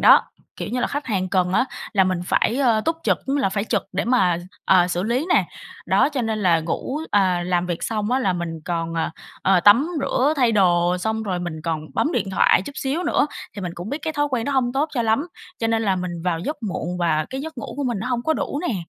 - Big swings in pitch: Yes, wide, 6.2 semitones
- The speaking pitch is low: No, high, 210 Hz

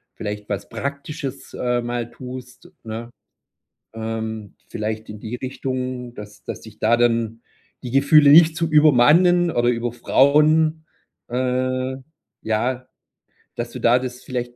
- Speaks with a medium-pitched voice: No, low, 125 Hz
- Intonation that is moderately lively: Yes, average, 3.2 semitones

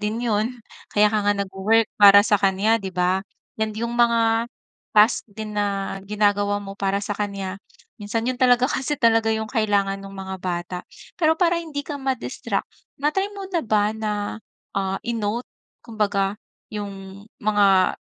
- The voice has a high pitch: Yes, high, 210 Hz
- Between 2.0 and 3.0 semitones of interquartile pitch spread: Yes, narrow, 2.5 semitones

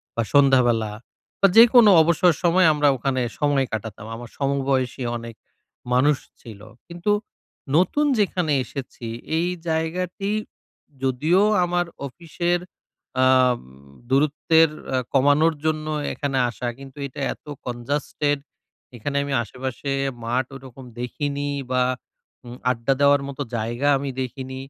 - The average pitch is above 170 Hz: No, medium, 140 Hz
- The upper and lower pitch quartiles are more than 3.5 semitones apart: Yes, average, 4.0 semitones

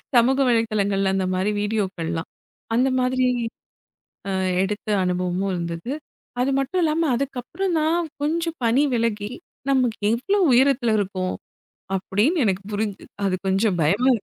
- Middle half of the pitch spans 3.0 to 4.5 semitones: No, wide, 5.5 semitones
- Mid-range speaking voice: No, high, 225 Hz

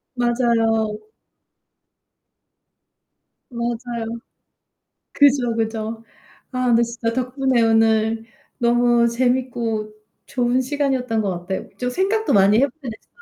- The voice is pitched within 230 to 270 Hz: Yes, high, 235 Hz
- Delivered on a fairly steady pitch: Yes, narrow, 2.1 semitones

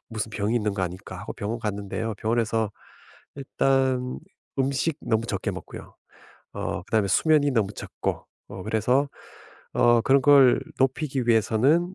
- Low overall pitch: Yes, low, 120 Hz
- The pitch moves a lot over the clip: No, average, 3.9 semitones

